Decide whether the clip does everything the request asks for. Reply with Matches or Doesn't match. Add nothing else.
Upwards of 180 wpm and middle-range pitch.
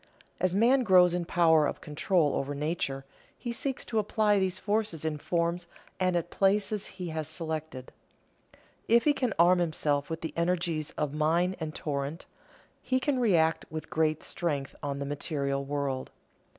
Doesn't match